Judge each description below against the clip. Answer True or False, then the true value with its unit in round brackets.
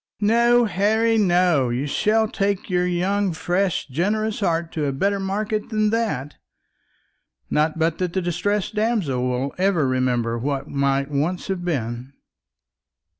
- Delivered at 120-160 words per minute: True (140 wpm)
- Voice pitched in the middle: True (180 Hz)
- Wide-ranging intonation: True (6.7 semitones)